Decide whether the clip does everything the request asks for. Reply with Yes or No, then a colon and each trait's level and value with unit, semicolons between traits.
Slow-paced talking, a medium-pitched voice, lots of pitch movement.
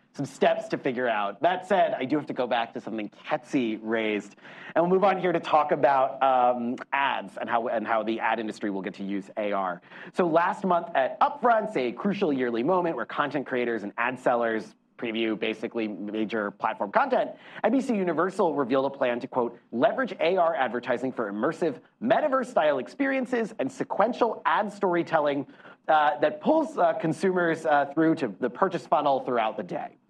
No: average, 180 wpm; medium, 145 Hz; wide, 7.9 semitones